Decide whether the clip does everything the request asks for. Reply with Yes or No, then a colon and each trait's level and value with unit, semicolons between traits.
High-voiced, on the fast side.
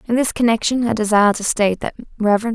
Yes: high, 225 Hz; fast, 210 wpm